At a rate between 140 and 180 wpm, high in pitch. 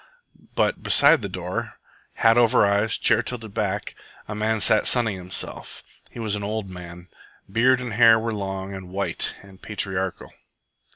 No: average, 160 wpm; low, 105 Hz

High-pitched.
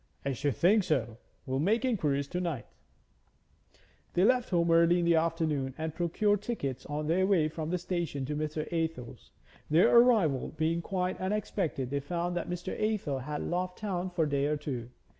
No: medium, 165 Hz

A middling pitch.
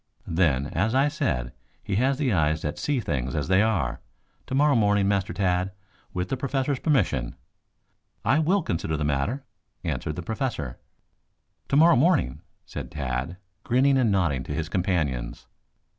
No: very low, 95 Hz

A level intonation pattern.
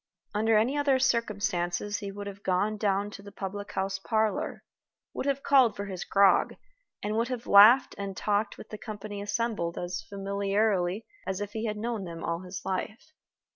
Yes: narrow, 2.1 semitones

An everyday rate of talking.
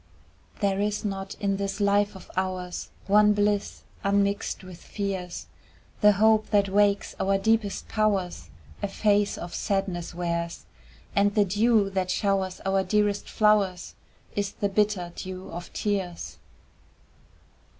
No: slow, 130 wpm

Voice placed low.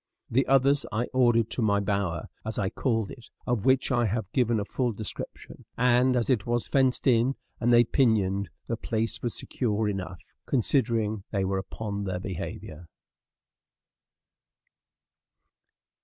Yes: low, 115 Hz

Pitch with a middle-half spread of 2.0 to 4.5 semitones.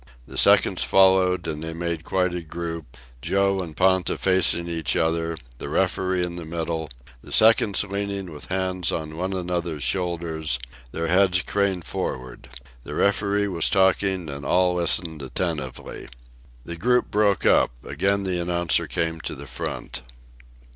Yes: narrow, 2.6 semitones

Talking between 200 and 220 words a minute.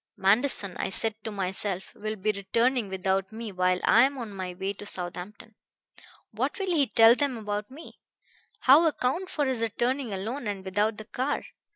No: average, 180 wpm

